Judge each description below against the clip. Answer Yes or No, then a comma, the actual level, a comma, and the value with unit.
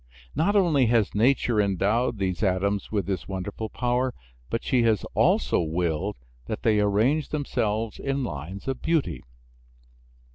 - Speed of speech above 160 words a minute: No, average, 140 wpm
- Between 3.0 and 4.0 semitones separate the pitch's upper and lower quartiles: No, average, 4.5 semitones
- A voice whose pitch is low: Yes, low, 110 Hz